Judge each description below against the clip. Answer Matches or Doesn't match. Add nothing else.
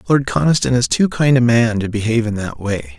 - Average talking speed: Doesn't match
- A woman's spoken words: Doesn't match